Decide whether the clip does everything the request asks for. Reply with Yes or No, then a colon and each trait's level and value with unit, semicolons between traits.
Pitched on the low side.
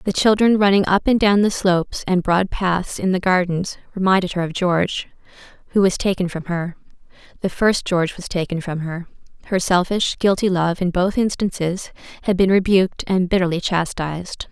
No: medium, 185 Hz